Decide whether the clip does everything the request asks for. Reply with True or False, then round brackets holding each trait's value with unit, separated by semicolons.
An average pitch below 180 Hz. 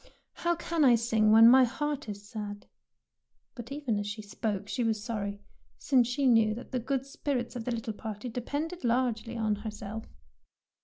False (230 Hz)